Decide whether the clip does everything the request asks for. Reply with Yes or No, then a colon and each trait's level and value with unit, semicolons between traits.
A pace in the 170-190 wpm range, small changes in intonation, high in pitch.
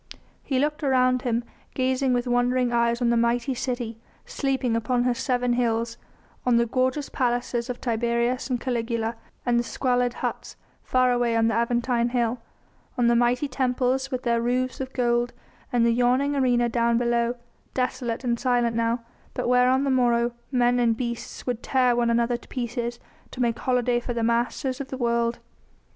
Yes: average, 180 wpm; narrow, 1.3 semitones; high, 245 Hz